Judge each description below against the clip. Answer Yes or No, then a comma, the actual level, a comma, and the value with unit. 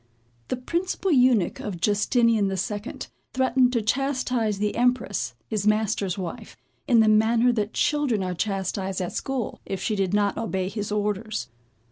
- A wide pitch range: No, average, 3.9 semitones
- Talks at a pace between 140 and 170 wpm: Yes, average, 155 wpm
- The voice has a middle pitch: No, high, 215 Hz